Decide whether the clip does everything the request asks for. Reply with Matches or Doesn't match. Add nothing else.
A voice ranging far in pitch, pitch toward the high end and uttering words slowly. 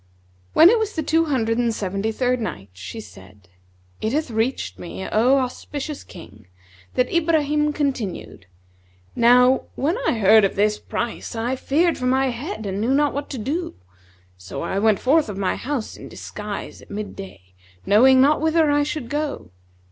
Doesn't match